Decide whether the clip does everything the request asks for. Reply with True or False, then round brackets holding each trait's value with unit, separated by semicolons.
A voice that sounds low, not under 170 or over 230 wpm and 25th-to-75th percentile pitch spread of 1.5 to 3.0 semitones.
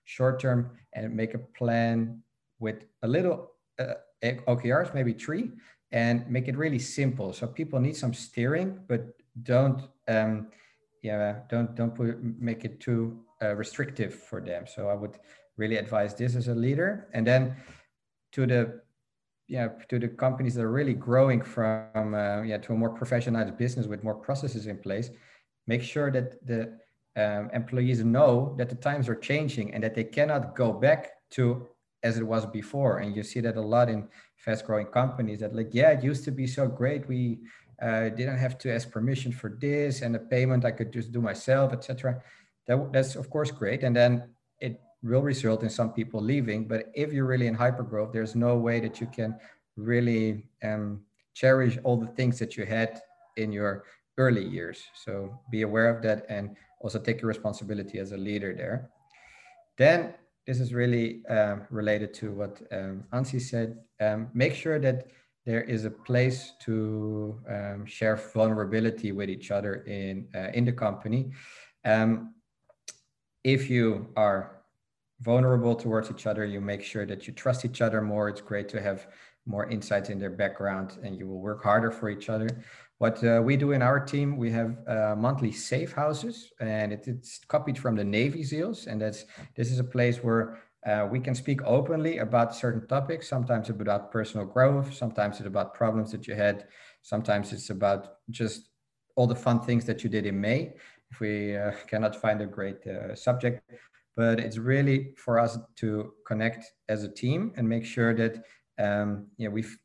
True (115 Hz; 185 wpm; 2.7 semitones)